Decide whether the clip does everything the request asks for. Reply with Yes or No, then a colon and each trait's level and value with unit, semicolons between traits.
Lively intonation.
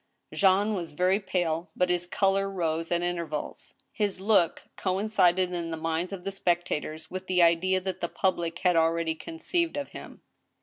No: narrow, 2.6 semitones